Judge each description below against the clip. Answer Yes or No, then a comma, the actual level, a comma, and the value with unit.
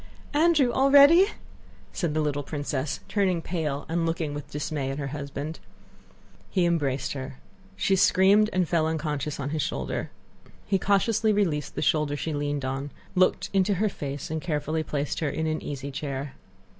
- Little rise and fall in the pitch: No, average, 4.5 semitones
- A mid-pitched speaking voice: Yes, medium, 155 Hz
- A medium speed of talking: Yes, average, 165 wpm